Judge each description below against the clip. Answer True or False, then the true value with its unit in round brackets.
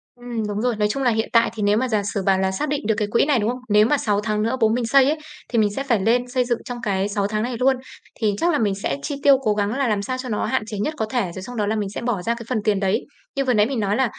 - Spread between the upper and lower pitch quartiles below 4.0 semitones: True (3.3 semitones)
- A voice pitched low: False (225 Hz)